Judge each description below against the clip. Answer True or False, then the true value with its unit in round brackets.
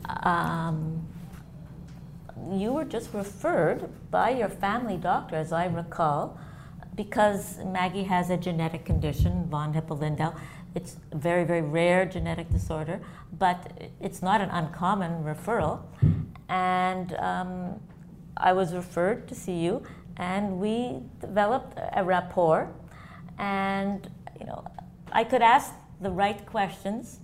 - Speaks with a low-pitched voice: False (180 Hz)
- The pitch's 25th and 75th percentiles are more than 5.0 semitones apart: False (3.1 semitones)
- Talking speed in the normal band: False (120 wpm)